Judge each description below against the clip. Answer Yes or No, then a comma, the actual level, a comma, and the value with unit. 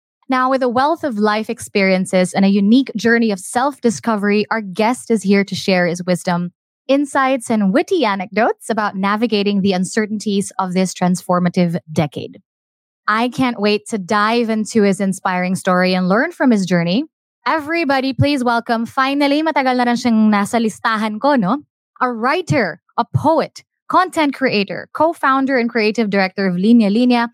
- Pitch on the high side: Yes, high, 220 Hz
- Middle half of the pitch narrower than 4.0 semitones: No, average, 4.6 semitones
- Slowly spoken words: No, average, 145 wpm